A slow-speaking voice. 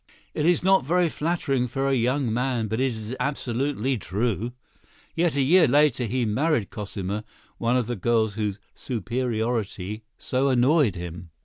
No: average, 155 wpm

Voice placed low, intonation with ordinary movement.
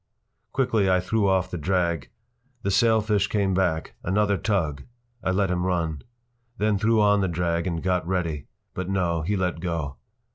Yes: very low, 95 Hz; average, 3.0 semitones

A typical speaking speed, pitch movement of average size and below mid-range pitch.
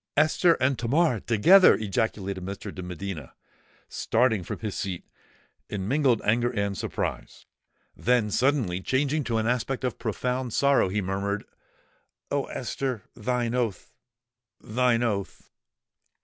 No: slow, 120 wpm; average, 4.1 semitones; low, 115 Hz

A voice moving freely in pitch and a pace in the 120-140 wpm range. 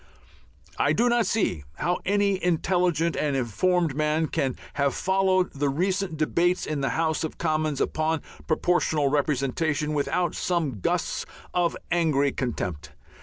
No: average, 3.9 semitones; slow, 135 wpm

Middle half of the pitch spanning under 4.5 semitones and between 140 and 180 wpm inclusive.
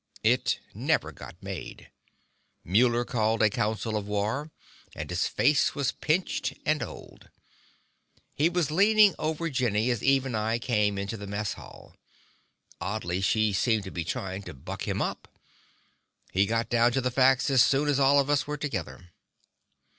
No: average, 5.3 semitones; average, 165 wpm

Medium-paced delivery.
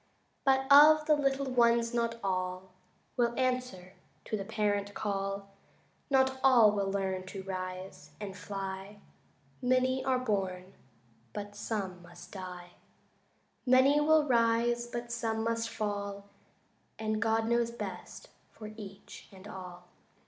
No: slow, 125 wpm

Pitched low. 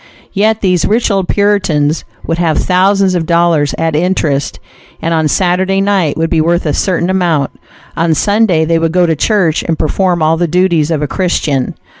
No: medium, 170 Hz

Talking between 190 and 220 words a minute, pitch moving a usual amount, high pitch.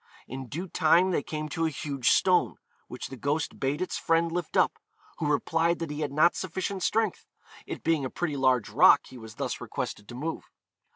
No: fast, 205 wpm; average, 3.8 semitones; medium, 155 Hz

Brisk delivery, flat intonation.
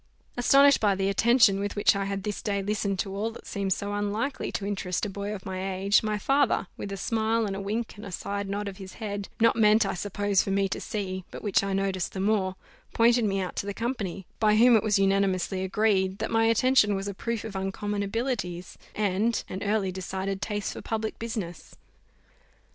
Yes: fast, 215 wpm; narrow, 2.1 semitones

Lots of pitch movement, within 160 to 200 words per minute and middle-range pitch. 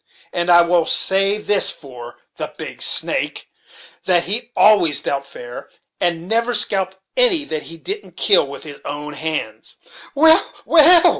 No: wide, 7.2 semitones; average, 150 wpm; medium, 180 Hz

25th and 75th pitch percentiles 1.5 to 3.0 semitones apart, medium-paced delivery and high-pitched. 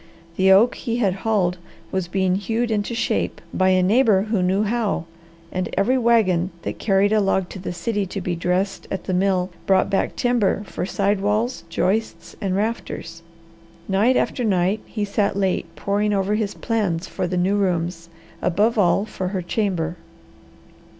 Yes: average, 2.7 semitones; average, 170 wpm; high, 195 Hz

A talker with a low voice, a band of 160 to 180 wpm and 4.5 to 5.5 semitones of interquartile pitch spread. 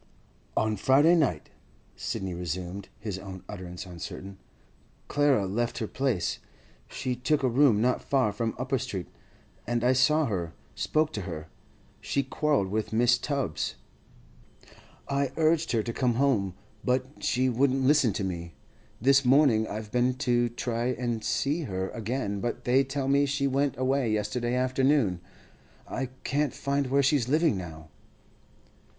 No: low, 125 Hz; average, 150 wpm; average, 5.0 semitones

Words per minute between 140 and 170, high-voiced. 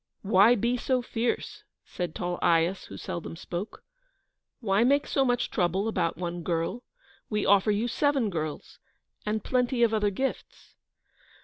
Yes: average, 145 wpm; high, 210 Hz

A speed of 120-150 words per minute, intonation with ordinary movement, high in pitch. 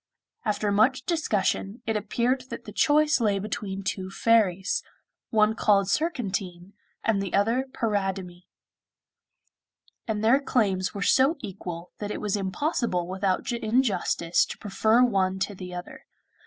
Yes: slow, 135 wpm; average, 3.6 semitones; high, 205 Hz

